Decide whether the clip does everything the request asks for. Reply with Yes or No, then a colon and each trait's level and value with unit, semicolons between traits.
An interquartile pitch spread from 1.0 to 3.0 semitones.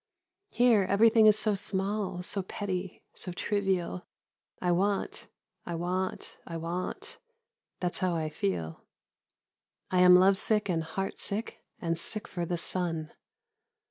Yes: average, 2.7 semitones